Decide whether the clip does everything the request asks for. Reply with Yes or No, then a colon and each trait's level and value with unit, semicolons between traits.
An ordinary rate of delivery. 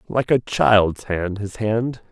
Yes: average, 170 wpm